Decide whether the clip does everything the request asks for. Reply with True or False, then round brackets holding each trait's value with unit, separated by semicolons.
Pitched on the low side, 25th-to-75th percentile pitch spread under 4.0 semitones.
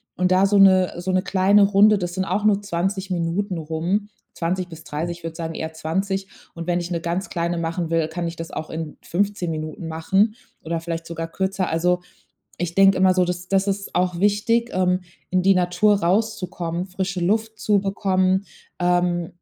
False (180 Hz; 2.5 semitones)